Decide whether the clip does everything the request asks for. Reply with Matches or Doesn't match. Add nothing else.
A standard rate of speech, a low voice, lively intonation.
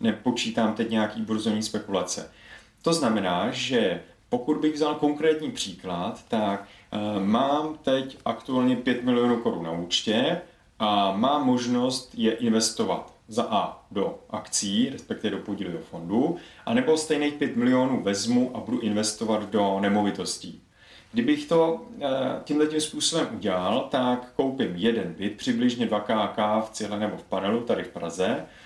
Matches